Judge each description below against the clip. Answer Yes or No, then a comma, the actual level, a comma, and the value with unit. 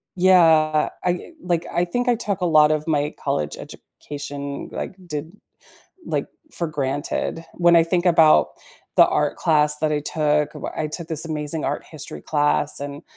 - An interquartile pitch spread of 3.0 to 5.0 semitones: No, narrow, 2.5 semitones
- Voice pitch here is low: No, medium, 155 Hz